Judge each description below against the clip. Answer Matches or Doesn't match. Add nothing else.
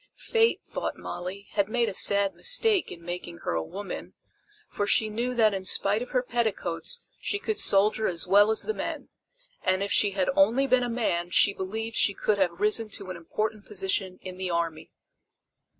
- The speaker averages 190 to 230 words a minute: Matches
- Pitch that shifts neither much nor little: Matches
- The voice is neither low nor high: Doesn't match